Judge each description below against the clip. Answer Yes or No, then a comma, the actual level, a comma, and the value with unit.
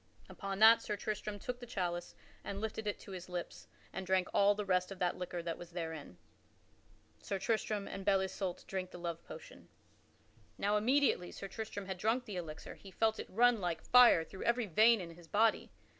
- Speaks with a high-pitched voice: Yes, high, 195 Hz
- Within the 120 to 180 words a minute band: No, fast, 205 wpm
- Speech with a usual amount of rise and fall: Yes, average, 3.6 semitones